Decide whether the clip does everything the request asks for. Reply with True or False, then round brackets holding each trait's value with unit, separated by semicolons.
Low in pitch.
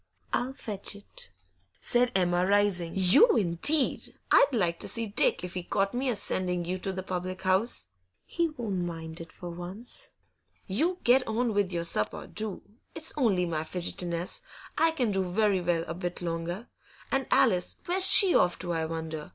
False (190 Hz)